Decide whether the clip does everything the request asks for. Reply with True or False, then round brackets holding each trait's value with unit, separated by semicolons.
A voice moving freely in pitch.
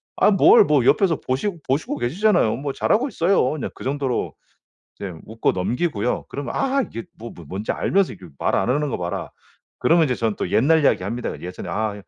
True (7.0 semitones)